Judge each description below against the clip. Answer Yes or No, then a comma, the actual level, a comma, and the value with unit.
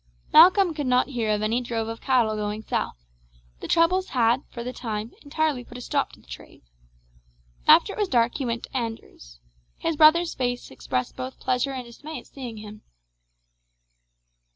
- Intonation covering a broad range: No, average, 4.9 semitones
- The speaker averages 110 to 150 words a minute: No, average, 175 wpm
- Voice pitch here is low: No, high, 245 Hz